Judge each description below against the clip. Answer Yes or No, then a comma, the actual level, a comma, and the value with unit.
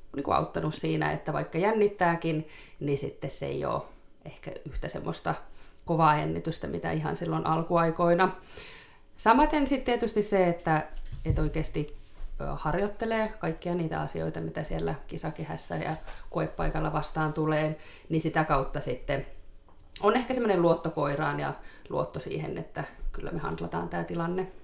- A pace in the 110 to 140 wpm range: Yes, average, 130 wpm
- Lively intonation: Yes, wide, 7.7 semitones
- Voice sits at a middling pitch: Yes, medium, 155 Hz